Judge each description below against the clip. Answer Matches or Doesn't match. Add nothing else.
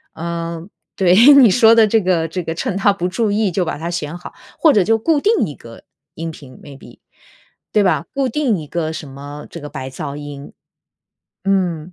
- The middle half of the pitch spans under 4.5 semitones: Doesn't match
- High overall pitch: Doesn't match